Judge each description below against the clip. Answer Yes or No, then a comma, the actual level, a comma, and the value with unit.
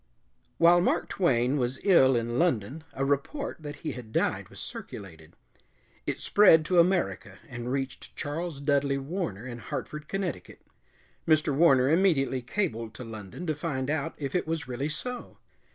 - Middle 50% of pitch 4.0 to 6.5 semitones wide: Yes, average, 5.1 semitones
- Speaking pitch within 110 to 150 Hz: Yes, medium, 140 Hz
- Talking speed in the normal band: Yes, average, 155 wpm